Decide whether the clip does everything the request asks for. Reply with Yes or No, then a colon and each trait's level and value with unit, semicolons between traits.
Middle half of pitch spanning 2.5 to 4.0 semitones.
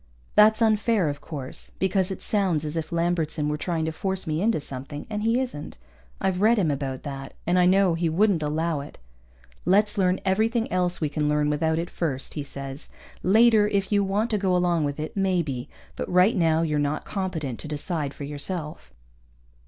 No: average, 4.6 semitones